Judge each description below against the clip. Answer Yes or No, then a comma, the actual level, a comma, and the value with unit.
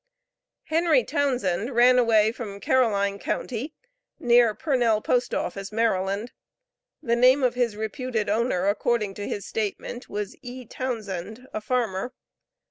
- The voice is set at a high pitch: Yes, high, 230 Hz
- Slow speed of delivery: Yes, slow, 125 wpm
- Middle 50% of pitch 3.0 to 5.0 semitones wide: Yes, average, 3.3 semitones